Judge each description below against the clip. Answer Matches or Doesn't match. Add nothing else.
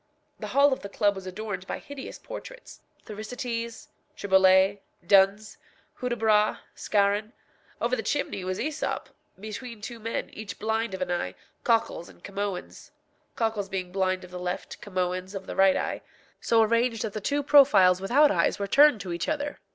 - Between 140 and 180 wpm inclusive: Matches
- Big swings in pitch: Doesn't match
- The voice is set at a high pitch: Matches